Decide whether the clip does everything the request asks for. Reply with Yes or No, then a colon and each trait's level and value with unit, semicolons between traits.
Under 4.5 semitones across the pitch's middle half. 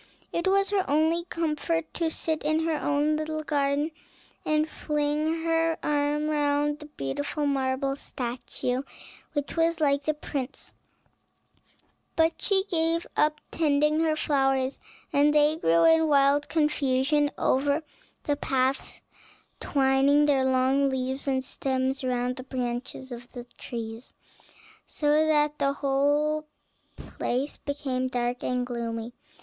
Yes: average, 2.7 semitones